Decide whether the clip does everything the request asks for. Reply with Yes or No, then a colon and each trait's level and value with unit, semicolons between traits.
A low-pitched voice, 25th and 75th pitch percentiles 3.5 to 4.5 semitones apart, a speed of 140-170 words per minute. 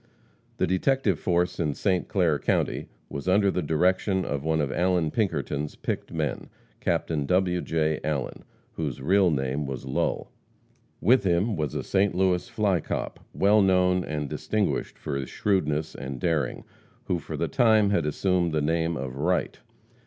Yes: very low, 85 Hz; average, 4.2 semitones; average, 160 wpm